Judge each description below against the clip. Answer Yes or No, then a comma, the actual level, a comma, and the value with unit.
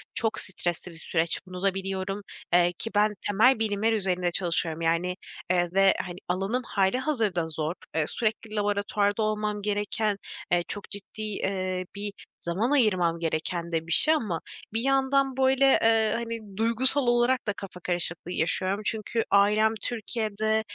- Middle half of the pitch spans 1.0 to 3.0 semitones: No, average, 3.8 semitones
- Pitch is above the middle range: Yes, high, 205 Hz